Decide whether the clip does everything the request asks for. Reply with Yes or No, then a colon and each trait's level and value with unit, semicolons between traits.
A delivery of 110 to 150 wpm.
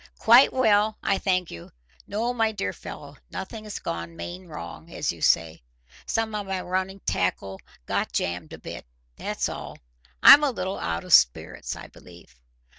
No: average, 165 wpm